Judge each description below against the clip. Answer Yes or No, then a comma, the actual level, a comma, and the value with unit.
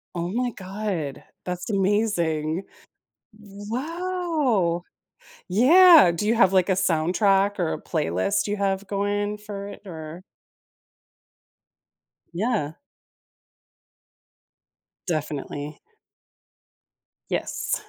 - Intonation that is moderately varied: Yes, average, 3.9 semitones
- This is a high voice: Yes, high, 200 Hz